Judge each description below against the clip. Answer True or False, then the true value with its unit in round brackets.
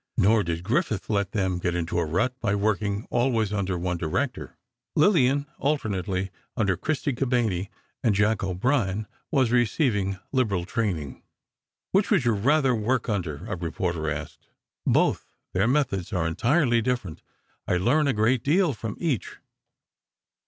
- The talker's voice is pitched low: True (105 Hz)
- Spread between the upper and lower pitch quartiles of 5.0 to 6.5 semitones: True (5.6 semitones)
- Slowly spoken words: False (145 wpm)